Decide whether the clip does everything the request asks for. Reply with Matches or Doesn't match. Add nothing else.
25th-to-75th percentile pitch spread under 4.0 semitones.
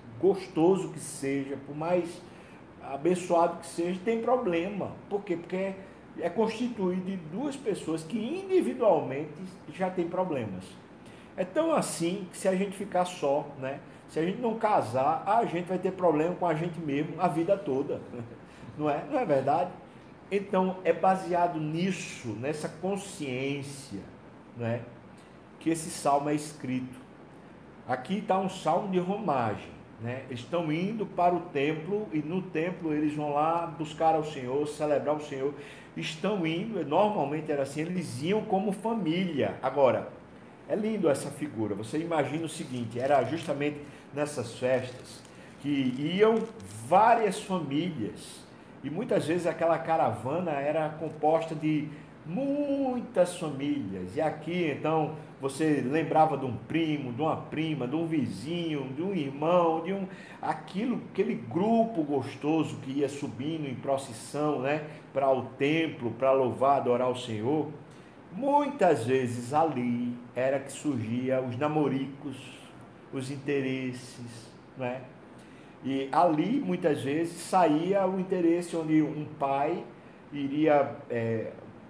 Doesn't match